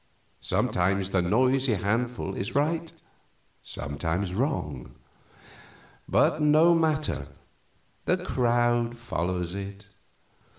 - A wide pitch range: Yes, wide, 6.5 semitones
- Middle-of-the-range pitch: No, low, 115 Hz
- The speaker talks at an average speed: No, slow, 85 wpm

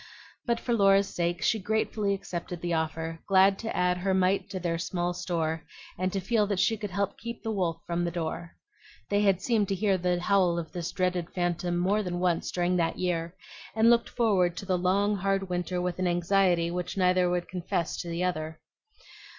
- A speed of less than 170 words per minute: No, fast, 205 wpm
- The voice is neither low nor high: Yes, medium, 180 Hz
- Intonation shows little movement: Yes, narrow, 2.2 semitones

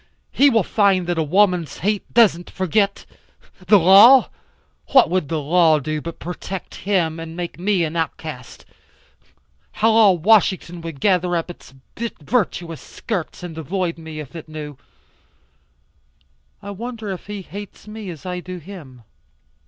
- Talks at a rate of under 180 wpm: Yes, average, 150 wpm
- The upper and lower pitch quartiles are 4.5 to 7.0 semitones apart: No, average, 3.8 semitones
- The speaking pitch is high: No, medium, 180 Hz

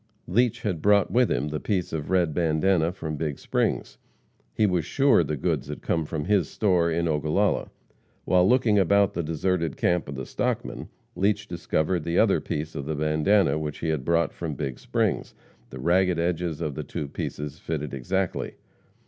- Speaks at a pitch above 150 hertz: No, very low, 85 Hz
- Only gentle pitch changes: No, average, 3.6 semitones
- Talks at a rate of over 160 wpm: Yes, average, 180 wpm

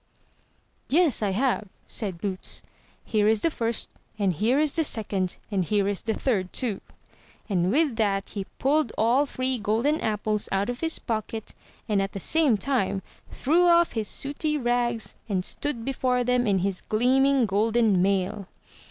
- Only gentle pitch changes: No, average, 4.8 semitones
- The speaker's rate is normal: Yes, average, 165 wpm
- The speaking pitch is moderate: No, high, 225 Hz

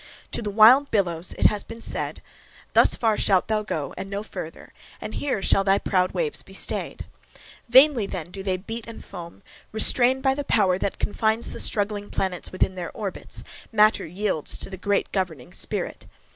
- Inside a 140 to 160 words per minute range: No, average, 185 wpm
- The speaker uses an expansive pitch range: No, average, 3.2 semitones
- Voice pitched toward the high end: Yes, high, 205 Hz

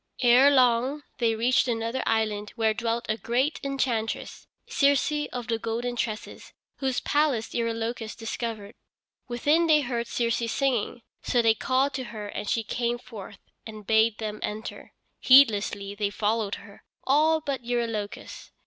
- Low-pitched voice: No, high, 235 Hz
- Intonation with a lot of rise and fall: No, average, 2.9 semitones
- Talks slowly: No, average, 145 wpm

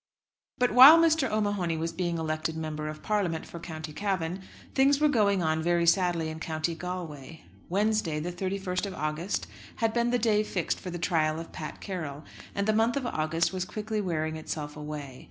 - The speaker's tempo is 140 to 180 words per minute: No, average, 190 wpm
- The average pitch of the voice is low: No, medium, 175 Hz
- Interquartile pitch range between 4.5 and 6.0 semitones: Yes, average, 4.8 semitones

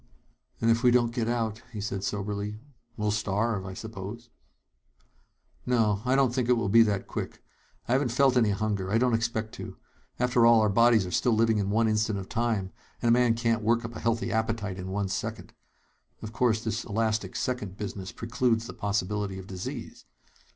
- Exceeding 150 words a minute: Yes, average, 195 wpm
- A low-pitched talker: Yes, low, 110 Hz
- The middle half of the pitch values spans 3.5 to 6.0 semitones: No, narrow, 2.4 semitones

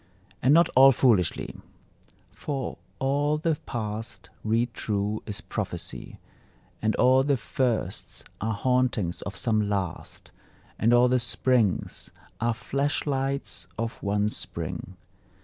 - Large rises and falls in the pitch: No, average, 3.9 semitones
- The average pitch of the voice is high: No, low, 120 Hz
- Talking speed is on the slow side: Yes, slow, 120 wpm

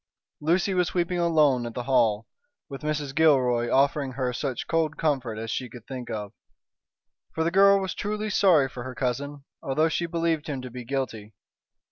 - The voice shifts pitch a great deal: No, average, 4.8 semitones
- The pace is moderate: Yes, average, 180 wpm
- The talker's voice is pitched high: No, medium, 140 Hz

